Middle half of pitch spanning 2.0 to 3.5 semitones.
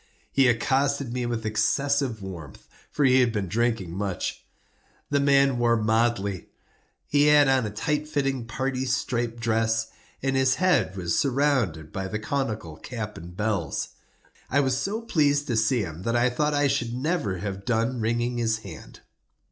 No: average, 4.3 semitones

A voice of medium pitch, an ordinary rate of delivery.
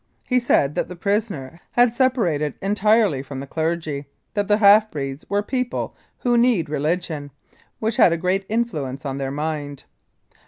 Yes: medium, 170 Hz; average, 160 wpm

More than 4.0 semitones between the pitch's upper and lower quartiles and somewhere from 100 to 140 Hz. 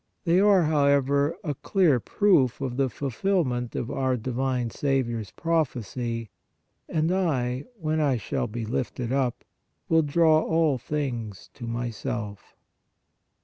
Yes: average, 4.6 semitones; low, 135 Hz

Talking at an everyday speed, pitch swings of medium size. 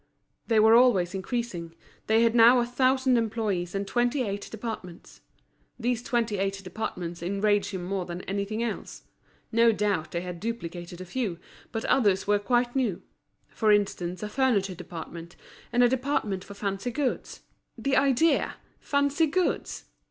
Yes: average, 150 wpm; average, 4.4 semitones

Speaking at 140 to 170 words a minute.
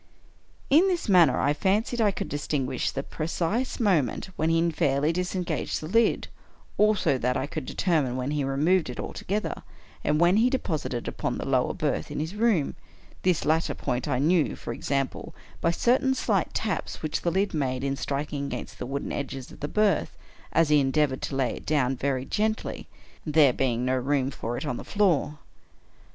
No: average, 190 wpm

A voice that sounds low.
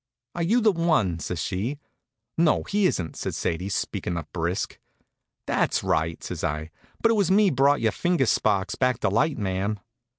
Yes: low, 115 Hz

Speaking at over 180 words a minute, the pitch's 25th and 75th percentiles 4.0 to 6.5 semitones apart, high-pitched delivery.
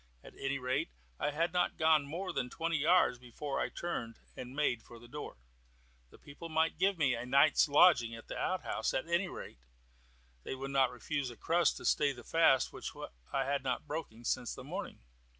No: average, 200 wpm; average, 4.5 semitones; medium, 140 Hz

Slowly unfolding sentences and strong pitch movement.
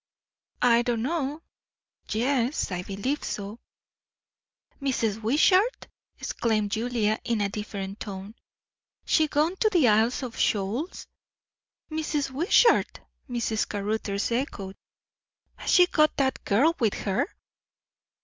Yes: slow, 110 wpm; wide, 5.7 semitones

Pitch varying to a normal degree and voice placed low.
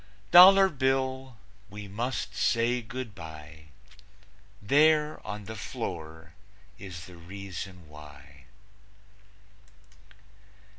No: wide, 8.0 semitones; low, 100 Hz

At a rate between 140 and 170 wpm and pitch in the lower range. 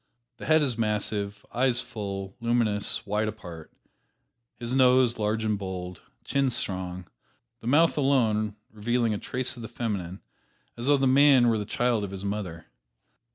Yes: average, 155 wpm; low, 110 Hz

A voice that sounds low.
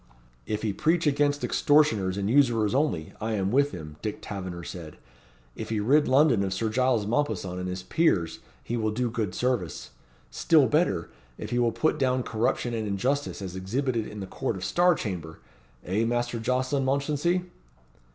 Yes: low, 115 Hz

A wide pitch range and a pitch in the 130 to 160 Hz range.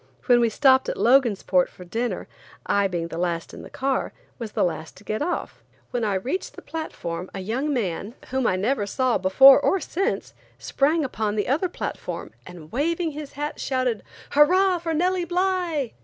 No: wide, 7.2 semitones; very high, 255 Hz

